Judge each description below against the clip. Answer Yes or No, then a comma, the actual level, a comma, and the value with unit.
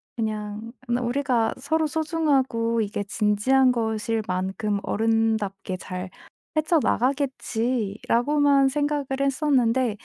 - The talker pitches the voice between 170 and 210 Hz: No, high, 235 Hz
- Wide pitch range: No, average, 4.4 semitones